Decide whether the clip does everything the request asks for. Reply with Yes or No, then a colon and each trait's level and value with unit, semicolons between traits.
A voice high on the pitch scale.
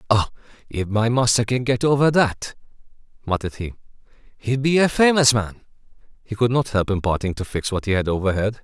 No: low, 115 Hz